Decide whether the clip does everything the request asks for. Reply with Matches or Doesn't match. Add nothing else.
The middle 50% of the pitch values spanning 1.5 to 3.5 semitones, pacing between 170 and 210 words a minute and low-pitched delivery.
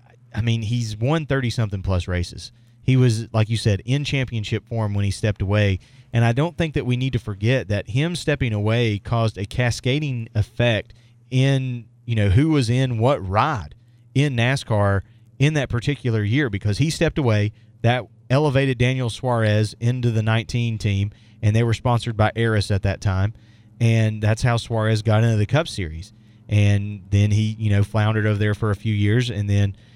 Matches